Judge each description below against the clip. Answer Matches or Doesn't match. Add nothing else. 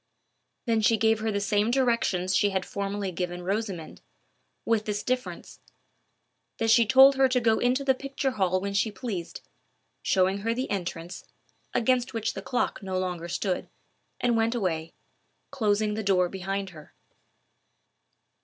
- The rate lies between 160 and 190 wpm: Doesn't match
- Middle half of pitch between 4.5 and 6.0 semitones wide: Doesn't match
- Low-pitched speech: Doesn't match